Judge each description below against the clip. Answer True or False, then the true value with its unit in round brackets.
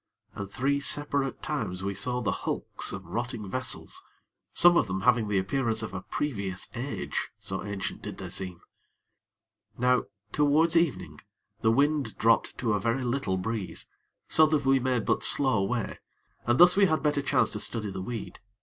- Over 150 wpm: True (175 wpm)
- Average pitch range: False (5.9 semitones)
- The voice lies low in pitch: True (120 Hz)